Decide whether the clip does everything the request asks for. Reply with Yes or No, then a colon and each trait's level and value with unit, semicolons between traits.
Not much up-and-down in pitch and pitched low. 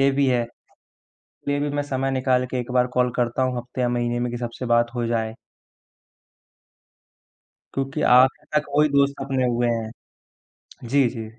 Yes: narrow, 2.1 semitones; low, 125 Hz